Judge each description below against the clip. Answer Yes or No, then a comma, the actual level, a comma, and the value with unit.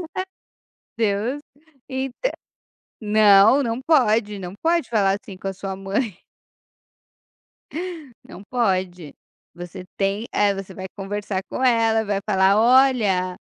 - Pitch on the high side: Yes, high, 205 Hz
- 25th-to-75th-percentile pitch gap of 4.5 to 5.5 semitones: No, average, 3.7 semitones